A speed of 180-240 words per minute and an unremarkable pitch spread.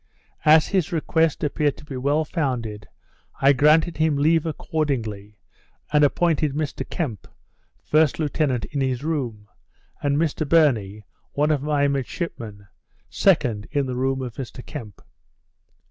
No: slow, 135 wpm; average, 3.8 semitones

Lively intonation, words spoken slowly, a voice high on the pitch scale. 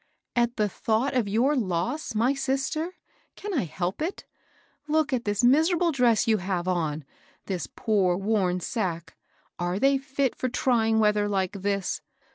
No: wide, 6.2 semitones; average, 170 wpm; high, 220 Hz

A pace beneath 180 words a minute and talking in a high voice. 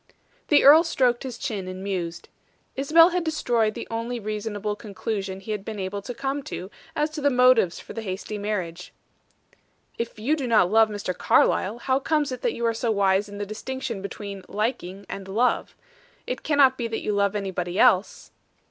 No: average, 190 wpm; high, 220 Hz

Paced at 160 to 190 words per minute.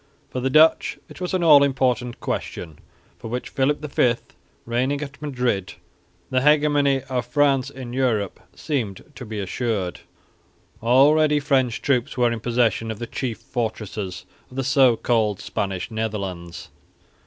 No: average, 145 wpm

